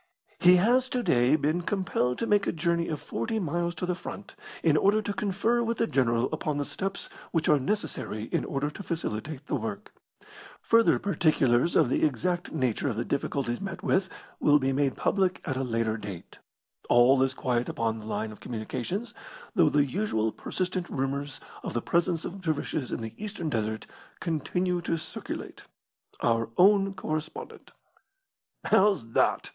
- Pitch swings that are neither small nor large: No, wide, 7.1 semitones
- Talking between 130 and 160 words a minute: No, average, 170 wpm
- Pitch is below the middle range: No, medium, 155 Hz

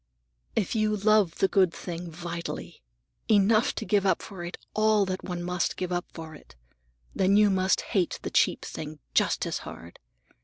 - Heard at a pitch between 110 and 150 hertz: No, medium, 185 Hz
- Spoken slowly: No, average, 180 wpm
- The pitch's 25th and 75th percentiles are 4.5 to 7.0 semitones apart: No, average, 3.2 semitones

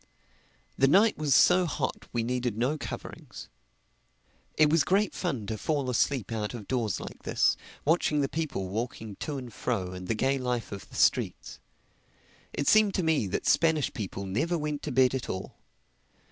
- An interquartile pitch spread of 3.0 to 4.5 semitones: No, wide, 5.5 semitones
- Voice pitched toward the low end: Yes, low, 130 Hz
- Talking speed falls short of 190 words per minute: Yes, average, 175 wpm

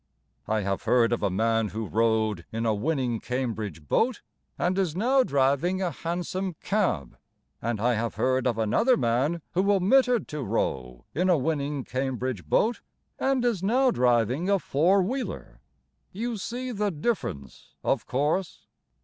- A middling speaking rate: Yes, average, 155 wpm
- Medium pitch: Yes, medium, 145 Hz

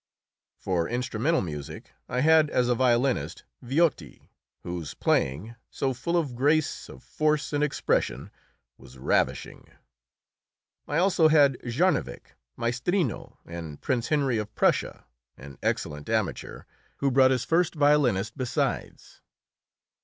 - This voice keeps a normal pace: No, slow, 120 wpm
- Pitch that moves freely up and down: Yes, wide, 6.1 semitones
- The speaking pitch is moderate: No, low, 130 Hz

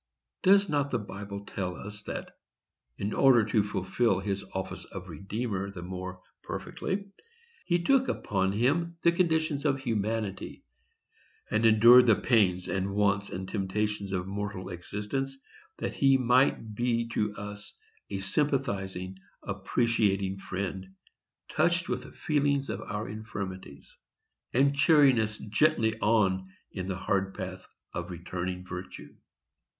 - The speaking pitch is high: No, low, 105 Hz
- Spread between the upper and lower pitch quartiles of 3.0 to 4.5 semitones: No, average, 4.9 semitones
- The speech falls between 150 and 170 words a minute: No, slow, 135 wpm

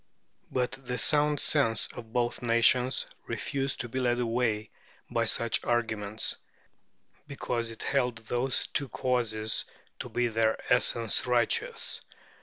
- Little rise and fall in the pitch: Yes, narrow, 2.0 semitones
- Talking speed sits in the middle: No, slow, 130 wpm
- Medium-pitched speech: No, low, 120 Hz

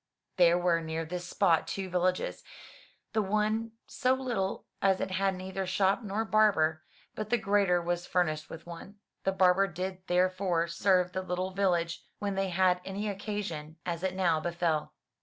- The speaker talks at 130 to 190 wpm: Yes, average, 170 wpm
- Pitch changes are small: Yes, narrow, 2.3 semitones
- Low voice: No, medium, 185 Hz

